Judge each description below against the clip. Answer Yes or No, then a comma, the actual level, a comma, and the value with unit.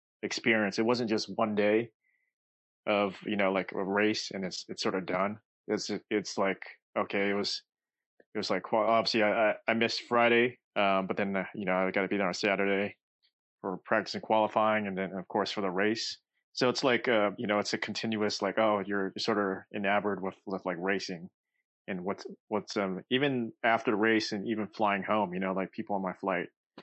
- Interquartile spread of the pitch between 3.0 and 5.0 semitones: No, narrow, 2.4 semitones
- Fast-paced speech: Yes, fast, 210 wpm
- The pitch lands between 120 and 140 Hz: No, low, 105 Hz